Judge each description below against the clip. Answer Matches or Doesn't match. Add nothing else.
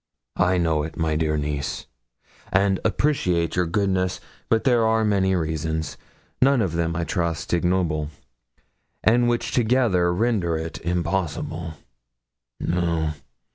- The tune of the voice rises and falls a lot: Doesn't match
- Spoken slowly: Matches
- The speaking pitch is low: Matches